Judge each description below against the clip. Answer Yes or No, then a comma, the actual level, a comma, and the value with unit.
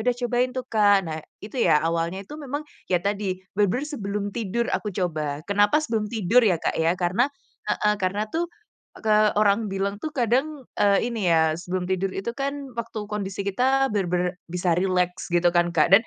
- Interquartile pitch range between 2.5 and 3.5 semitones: No, average, 4.7 semitones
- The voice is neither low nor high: No, high, 200 Hz